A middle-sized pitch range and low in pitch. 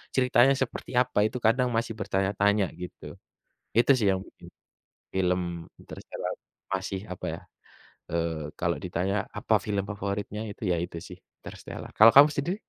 Yes: average, 4.3 semitones; low, 100 Hz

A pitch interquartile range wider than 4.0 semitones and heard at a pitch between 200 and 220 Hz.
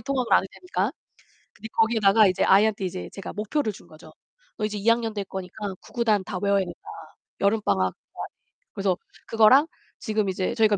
No: narrow, 2.4 semitones; high, 210 Hz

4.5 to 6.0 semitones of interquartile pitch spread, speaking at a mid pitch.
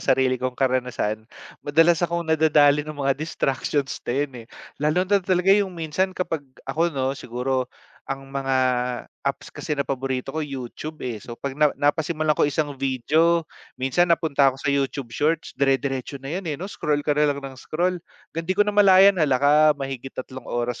No: average, 3.5 semitones; medium, 145 Hz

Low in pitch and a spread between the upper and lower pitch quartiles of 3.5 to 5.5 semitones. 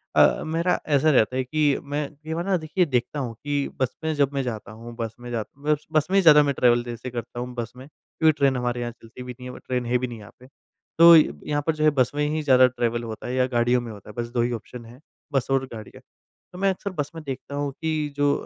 Yes: low, 130 Hz; average, 3.8 semitones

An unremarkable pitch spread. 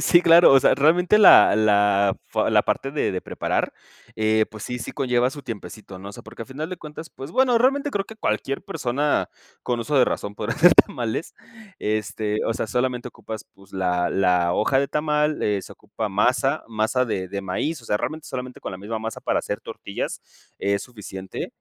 No: wide, 6.1 semitones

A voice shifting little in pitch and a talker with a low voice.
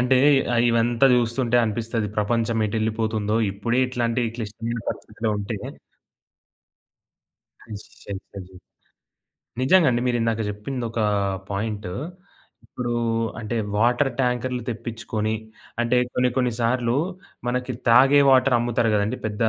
Yes: narrow, 2.1 semitones; low, 115 Hz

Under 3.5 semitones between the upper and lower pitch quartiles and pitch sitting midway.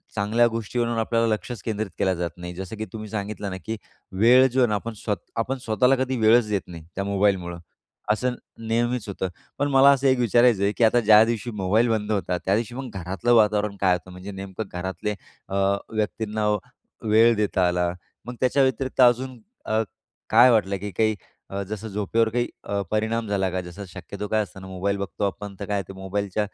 No: average, 3.0 semitones; low, 105 Hz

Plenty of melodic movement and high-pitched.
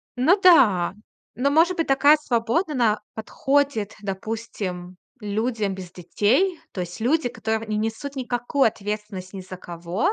Yes: wide, 5.8 semitones; high, 225 Hz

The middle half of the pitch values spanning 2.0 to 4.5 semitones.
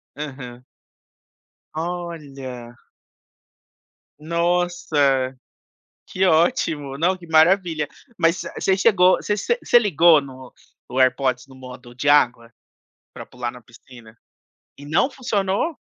No: wide, 5.5 semitones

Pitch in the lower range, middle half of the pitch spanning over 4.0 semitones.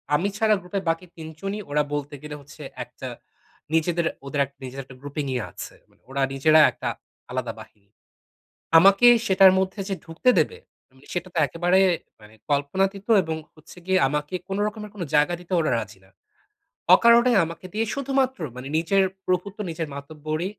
No: medium, 165 Hz; average, 4.9 semitones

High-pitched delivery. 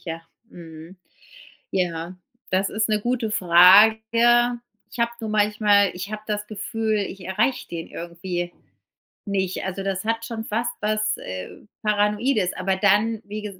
Yes: high, 210 Hz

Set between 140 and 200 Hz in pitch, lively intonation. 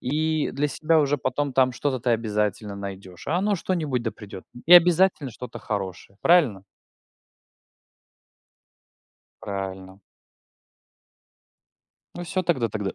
No: low, 125 Hz; wide, 7.7 semitones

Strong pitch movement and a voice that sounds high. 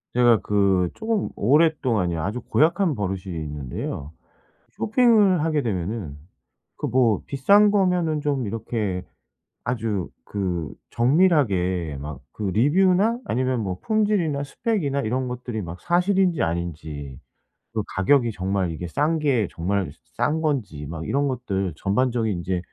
No: wide, 8.8 semitones; low, 115 Hz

